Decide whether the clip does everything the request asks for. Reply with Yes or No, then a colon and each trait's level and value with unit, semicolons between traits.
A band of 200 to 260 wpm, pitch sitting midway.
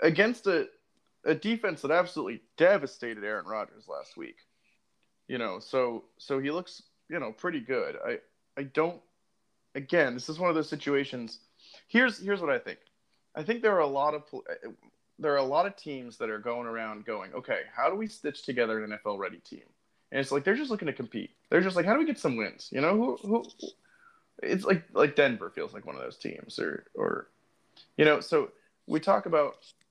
Yes: fast, 205 wpm; medium, 180 Hz